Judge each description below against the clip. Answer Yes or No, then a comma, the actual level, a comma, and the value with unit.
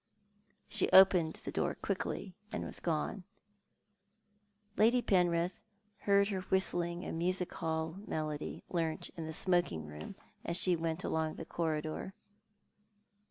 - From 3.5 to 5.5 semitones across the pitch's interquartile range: No, average, 2.8 semitones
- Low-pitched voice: No, medium, 170 Hz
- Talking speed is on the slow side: Yes, slow, 125 wpm